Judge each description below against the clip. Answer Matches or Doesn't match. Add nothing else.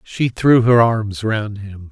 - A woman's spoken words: Doesn't match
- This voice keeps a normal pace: Matches